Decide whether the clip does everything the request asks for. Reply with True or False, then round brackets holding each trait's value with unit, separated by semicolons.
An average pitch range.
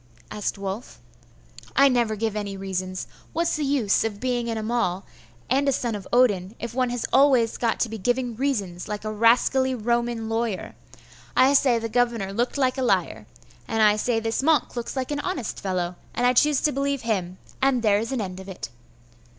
True (3.7 semitones)